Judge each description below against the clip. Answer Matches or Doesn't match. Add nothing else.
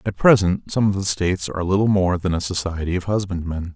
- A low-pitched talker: Matches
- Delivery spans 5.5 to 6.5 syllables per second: Matches